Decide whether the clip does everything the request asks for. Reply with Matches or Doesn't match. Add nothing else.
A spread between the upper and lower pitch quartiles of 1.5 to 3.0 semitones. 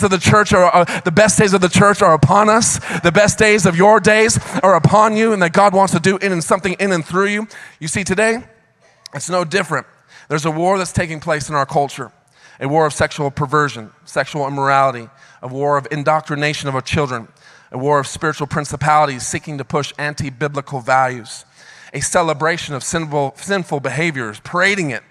Doesn't match